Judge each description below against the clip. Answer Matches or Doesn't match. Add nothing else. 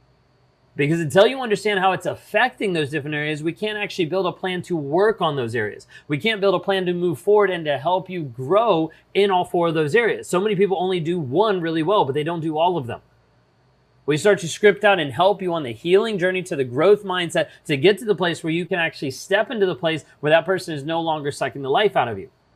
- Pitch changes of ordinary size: Matches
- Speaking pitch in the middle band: Matches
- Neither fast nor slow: Doesn't match